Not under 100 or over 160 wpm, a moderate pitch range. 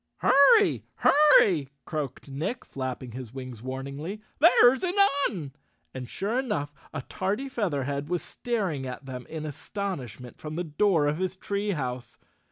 No: average, 150 wpm; wide, 7.5 semitones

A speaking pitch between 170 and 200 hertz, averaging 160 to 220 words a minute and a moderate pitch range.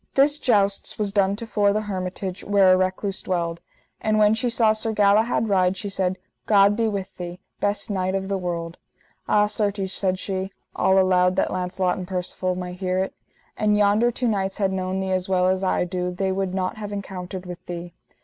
No: high, 190 Hz; fast, 205 wpm; narrow, 2.0 semitones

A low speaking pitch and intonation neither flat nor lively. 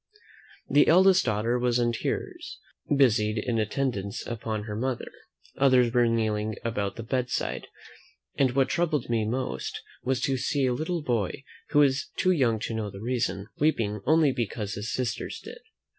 Yes: low, 120 Hz; average, 3.7 semitones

